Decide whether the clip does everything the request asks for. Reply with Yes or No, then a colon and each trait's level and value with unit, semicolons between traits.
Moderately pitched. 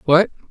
Yes: medium, 170 Hz